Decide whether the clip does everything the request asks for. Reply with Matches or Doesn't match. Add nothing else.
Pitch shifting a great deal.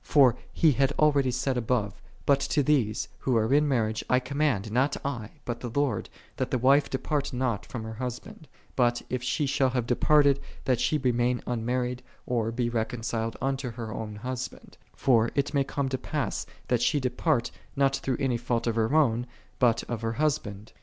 Doesn't match